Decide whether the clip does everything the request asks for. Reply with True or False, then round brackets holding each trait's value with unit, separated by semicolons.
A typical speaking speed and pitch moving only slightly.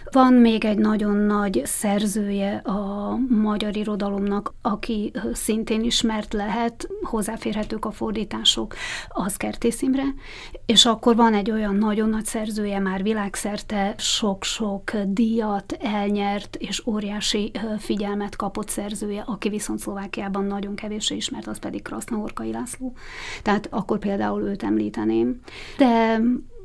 True (120 wpm; 2.1 semitones)